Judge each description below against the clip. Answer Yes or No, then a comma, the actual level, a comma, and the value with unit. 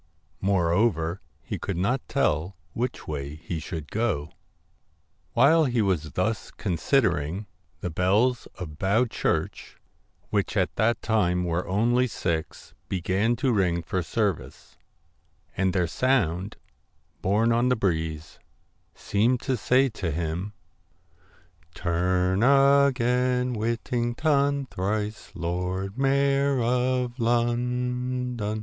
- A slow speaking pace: Yes, slow, 120 wpm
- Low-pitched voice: Yes, low, 105 Hz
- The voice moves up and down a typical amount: No, wide, 5.7 semitones